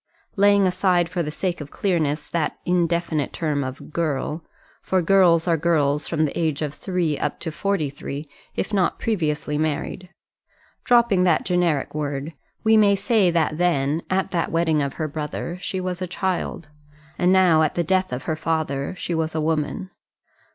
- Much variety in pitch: No, average, 3.3 semitones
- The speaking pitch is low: No, medium, 165 Hz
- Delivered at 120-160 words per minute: No, average, 175 wpm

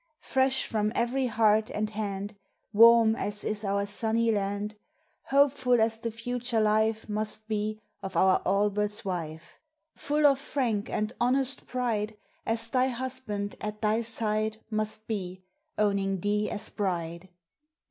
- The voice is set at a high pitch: Yes, high, 215 Hz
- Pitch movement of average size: No, narrow, 2.2 semitones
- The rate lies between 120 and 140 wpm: Yes, slow, 135 wpm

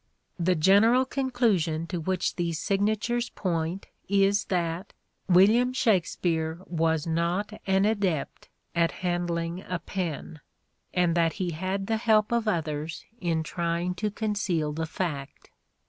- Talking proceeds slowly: Yes, slow, 130 wpm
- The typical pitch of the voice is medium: Yes, medium, 180 Hz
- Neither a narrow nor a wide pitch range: Yes, average, 3.5 semitones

